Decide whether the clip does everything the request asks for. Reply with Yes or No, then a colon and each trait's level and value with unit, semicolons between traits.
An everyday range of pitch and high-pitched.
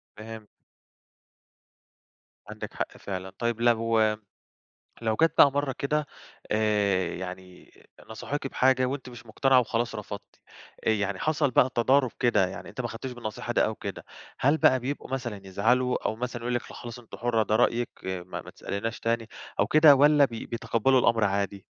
No: average, 3.5 semitones; low, 115 Hz